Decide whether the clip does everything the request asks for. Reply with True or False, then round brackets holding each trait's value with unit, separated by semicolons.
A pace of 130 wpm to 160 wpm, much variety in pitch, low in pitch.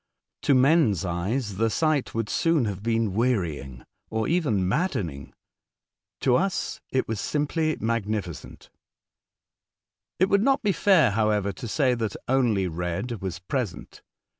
True (135 wpm; 6.8 semitones; 115 Hz)